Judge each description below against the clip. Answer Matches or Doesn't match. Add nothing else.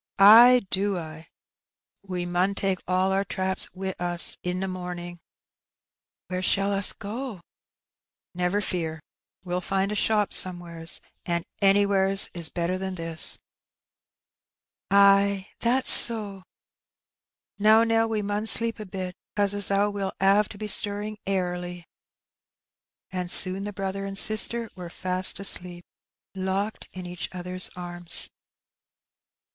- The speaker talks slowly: Matches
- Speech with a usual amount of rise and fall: Doesn't match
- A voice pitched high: Matches